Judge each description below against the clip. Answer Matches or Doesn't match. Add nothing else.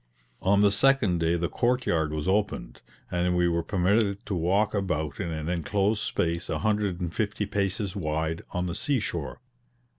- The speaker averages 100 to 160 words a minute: Doesn't match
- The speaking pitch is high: Doesn't match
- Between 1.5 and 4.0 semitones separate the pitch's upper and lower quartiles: Matches